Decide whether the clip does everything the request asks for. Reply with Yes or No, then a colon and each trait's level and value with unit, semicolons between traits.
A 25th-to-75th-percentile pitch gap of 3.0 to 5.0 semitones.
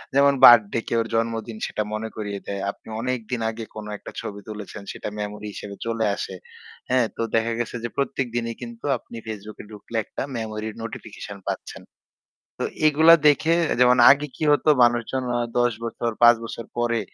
No: narrow, 2.5 semitones